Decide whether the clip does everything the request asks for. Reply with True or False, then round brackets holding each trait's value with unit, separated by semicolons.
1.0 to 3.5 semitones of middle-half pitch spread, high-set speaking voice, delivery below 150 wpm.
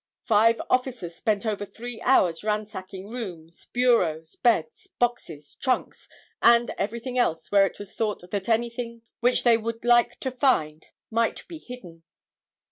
False (4.3 semitones; 225 Hz; 140 wpm)